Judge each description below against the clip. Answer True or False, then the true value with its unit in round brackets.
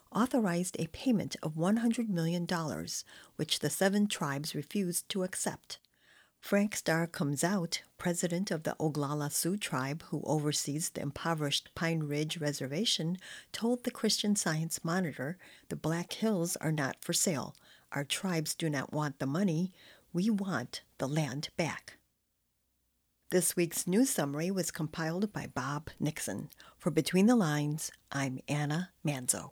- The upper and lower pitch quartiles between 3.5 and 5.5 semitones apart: True (4.3 semitones)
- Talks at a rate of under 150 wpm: True (140 wpm)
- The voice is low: False (165 Hz)